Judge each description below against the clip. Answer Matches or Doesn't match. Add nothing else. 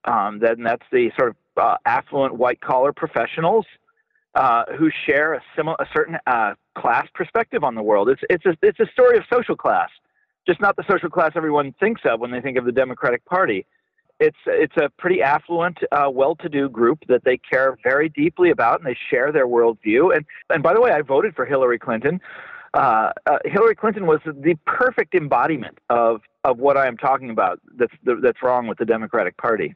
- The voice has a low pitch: Doesn't match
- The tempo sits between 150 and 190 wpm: Doesn't match